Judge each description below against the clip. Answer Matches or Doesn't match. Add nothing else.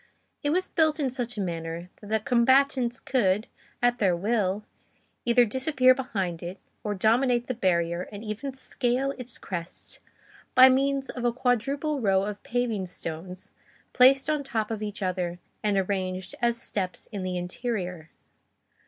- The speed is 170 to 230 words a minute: Doesn't match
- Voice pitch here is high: Matches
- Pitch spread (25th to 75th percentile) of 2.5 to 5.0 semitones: Doesn't match